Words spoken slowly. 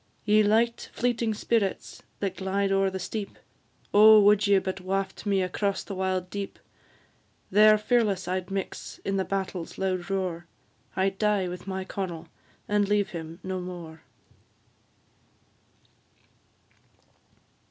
Yes: slow, 130 wpm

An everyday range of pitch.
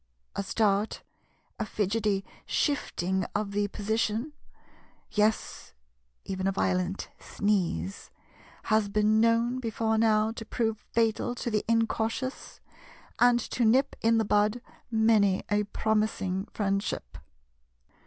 No: narrow, 2.1 semitones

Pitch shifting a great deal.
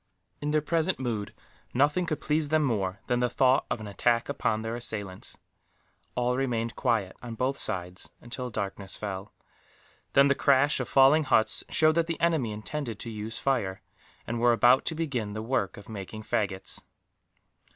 No: average, 4.7 semitones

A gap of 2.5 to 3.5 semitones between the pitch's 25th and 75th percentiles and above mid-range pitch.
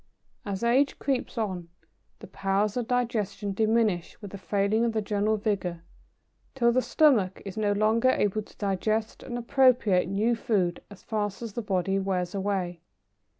Yes: average, 3.0 semitones; high, 210 Hz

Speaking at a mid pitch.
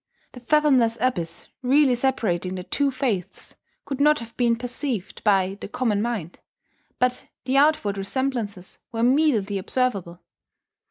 No: high, 235 Hz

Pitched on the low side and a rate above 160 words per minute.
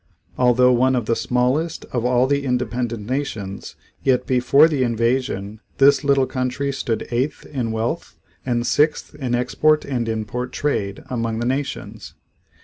No: low, 125 Hz; average, 145 wpm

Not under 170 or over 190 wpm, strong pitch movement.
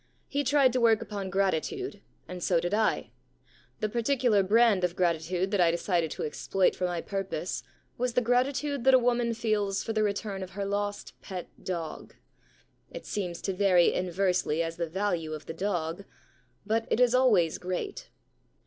No: average, 175 wpm; average, 4.4 semitones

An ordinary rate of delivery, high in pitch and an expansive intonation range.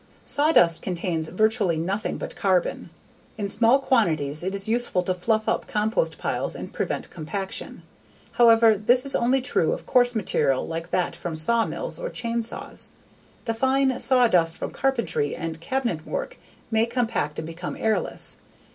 Yes: average, 160 wpm; high, 215 Hz; wide, 6.0 semitones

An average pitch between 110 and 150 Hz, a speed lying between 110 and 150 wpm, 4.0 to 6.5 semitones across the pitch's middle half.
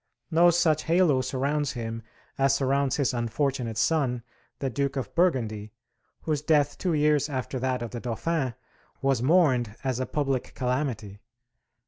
No: low, 135 Hz; average, 145 wpm; average, 3.5 semitones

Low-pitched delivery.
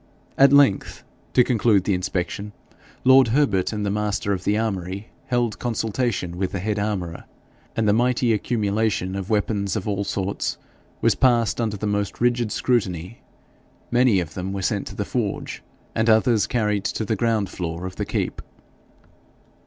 Yes: low, 105 Hz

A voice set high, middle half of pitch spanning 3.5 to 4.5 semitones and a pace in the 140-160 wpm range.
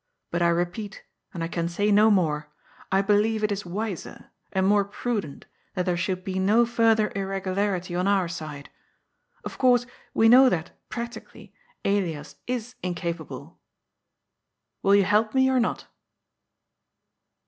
Yes: high, 195 Hz; average, 3.8 semitones; average, 145 wpm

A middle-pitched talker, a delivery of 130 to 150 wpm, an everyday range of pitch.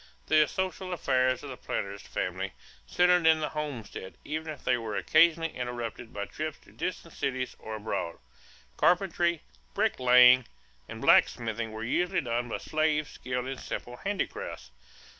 No: low, 130 Hz; average, 145 wpm; average, 5.0 semitones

